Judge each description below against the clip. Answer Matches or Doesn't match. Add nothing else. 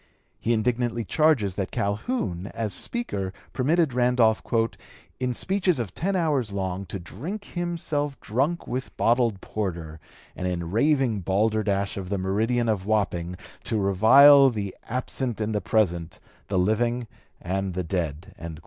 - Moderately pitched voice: Doesn't match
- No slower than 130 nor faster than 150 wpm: Matches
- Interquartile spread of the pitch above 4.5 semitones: Matches